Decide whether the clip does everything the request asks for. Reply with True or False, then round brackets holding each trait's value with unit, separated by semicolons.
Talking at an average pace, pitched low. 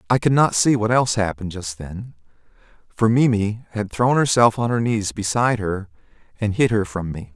True (195 wpm; 110 Hz)